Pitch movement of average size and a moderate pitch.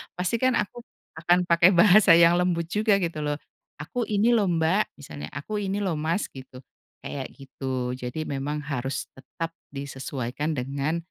No: wide, 5.7 semitones; medium, 165 Hz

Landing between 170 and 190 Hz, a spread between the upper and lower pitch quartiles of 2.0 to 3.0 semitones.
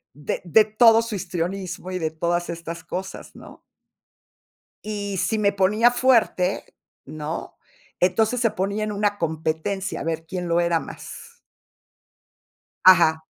No: medium, 185 Hz; average, 4.0 semitones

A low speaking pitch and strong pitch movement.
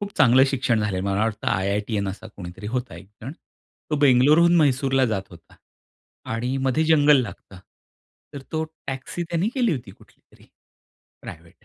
Yes: low, 125 Hz; wide, 6.3 semitones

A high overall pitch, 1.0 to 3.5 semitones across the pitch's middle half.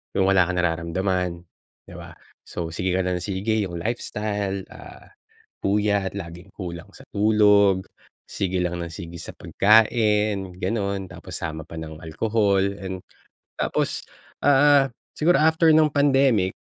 No: low, 100 Hz; average, 3.2 semitones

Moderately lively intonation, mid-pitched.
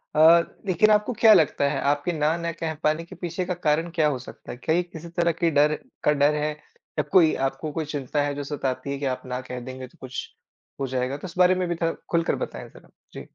Yes: average, 3.3 semitones; medium, 155 Hz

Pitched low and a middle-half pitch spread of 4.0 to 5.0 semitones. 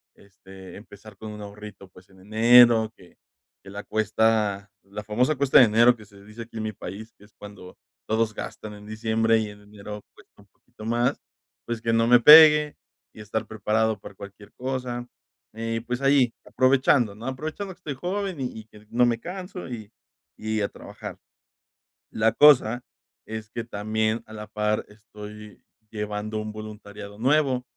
No: low, 110 Hz; narrow, 2.6 semitones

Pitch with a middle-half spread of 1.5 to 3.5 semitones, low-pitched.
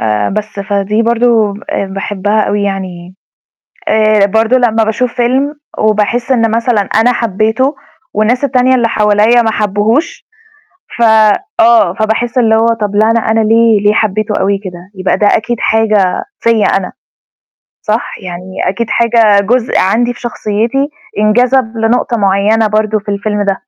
No: narrow, 2.4 semitones; high, 220 Hz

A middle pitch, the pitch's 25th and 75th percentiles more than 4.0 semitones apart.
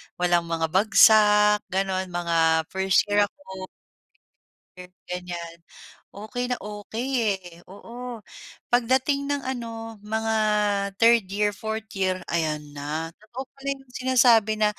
No: high, 210 Hz; average, 4.5 semitones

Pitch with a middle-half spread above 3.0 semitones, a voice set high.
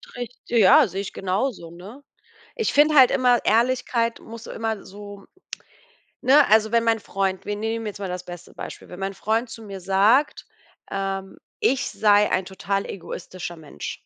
Yes: average, 3.4 semitones; high, 210 Hz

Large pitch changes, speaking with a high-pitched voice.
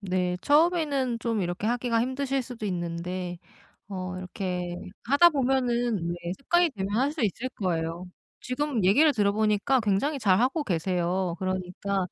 Yes: wide, 6.2 semitones; high, 205 Hz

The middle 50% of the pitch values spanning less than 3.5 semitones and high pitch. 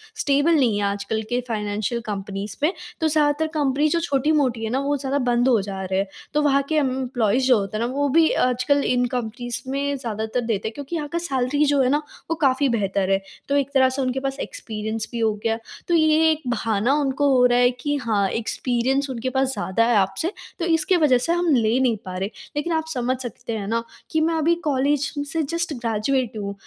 No: average, 4.4 semitones; very high, 255 Hz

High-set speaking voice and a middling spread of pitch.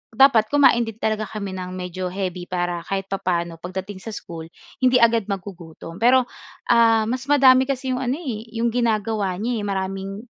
Yes: high, 215 Hz; average, 4.2 semitones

